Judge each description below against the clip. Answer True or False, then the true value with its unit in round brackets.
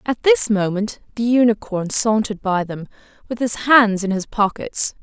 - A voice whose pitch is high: True (215 Hz)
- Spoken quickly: False (165 wpm)